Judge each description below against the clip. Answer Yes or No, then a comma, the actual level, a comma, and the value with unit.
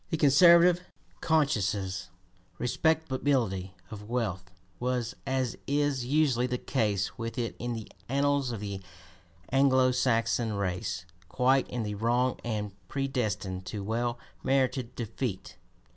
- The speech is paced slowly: Yes, slow, 120 wpm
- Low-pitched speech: Yes, low, 120 Hz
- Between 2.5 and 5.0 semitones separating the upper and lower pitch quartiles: Yes, average, 4.4 semitones